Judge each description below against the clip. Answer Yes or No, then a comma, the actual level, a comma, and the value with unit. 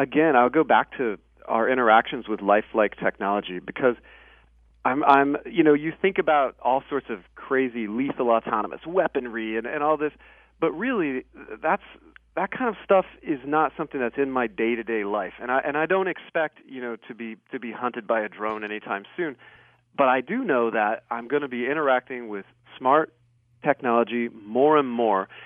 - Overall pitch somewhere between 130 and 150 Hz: No, low, 120 Hz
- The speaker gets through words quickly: No, average, 190 wpm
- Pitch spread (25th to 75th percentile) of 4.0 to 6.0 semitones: Yes, average, 4.7 semitones